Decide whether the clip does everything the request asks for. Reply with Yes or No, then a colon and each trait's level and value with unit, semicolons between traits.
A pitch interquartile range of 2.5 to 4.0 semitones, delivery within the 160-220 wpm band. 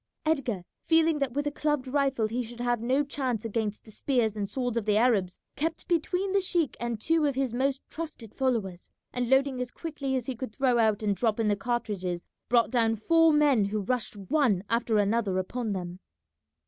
No: average, 4.4 semitones; average, 200 wpm